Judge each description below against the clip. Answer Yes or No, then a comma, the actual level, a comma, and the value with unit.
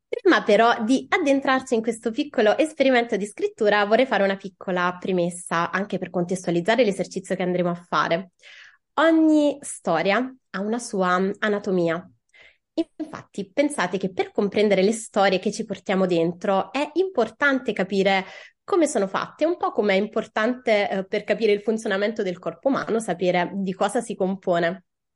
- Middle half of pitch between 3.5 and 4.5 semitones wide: Yes, average, 4.1 semitones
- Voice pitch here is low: No, high, 205 Hz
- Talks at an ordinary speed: Yes, average, 150 wpm